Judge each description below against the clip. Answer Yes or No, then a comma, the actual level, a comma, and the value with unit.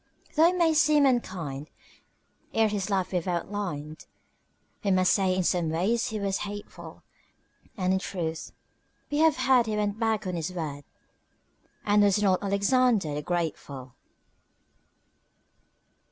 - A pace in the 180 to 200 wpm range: No, average, 140 wpm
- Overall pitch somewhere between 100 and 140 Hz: No, high, 195 Hz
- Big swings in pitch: No, average, 4.3 semitones